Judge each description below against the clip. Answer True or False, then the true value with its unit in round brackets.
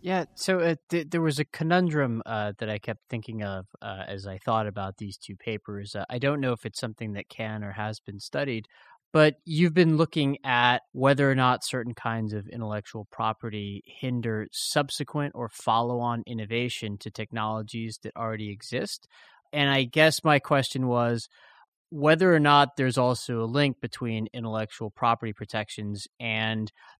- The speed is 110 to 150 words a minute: False (170 wpm)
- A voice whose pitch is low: True (115 Hz)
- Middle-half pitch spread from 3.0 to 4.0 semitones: False (4.4 semitones)